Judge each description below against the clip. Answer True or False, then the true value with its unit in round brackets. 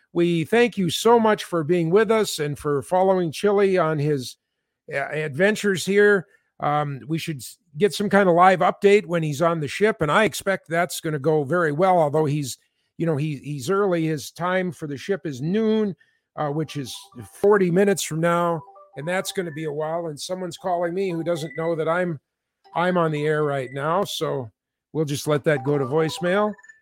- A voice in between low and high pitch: True (170 Hz)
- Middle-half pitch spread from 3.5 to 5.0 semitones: True (4.2 semitones)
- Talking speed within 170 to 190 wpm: False (205 wpm)